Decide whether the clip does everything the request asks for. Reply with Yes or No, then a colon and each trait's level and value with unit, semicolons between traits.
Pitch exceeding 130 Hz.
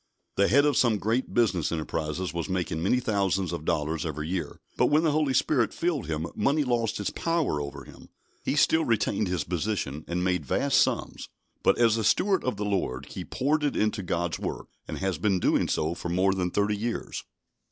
No: low, 100 Hz